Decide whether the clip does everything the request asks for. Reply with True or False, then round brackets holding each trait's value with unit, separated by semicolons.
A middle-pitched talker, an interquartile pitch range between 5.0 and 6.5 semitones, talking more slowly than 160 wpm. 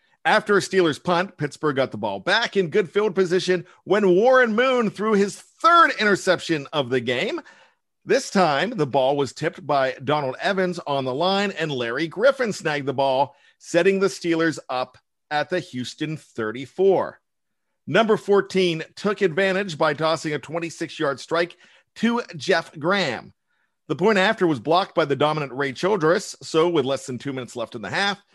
False (170 Hz; 5.4 semitones; 175 wpm)